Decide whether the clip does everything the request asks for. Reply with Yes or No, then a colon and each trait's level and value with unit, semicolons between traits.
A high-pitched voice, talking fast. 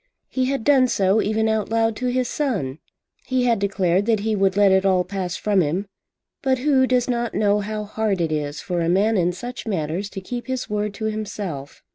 Yes: high, 210 Hz; fast, 215 wpm